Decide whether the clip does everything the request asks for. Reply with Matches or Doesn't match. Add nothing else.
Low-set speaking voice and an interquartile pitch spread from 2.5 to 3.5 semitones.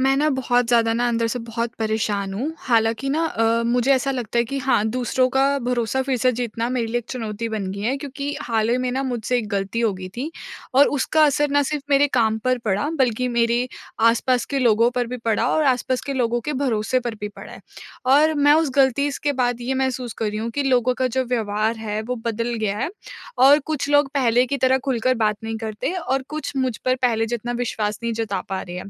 Doesn't match